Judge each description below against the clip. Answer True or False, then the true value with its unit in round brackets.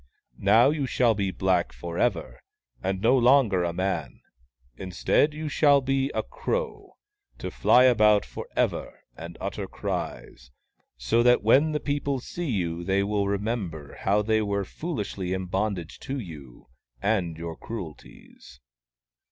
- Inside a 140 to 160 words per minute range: True (150 wpm)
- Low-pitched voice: True (105 Hz)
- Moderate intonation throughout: False (6.3 semitones)